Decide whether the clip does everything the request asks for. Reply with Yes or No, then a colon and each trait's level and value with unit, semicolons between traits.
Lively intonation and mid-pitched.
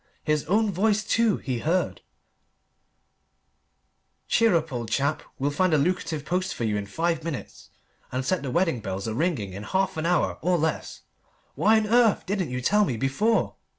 Yes: wide, 6.4 semitones; medium, 165 Hz